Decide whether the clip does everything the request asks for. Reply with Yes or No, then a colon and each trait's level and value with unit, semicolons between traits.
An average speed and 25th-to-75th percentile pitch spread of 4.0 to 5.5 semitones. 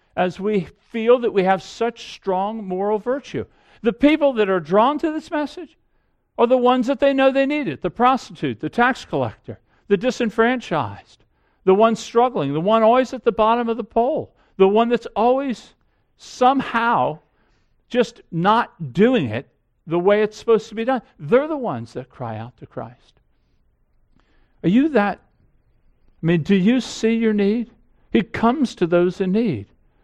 Yes: average, 170 wpm; average, 4.5 semitones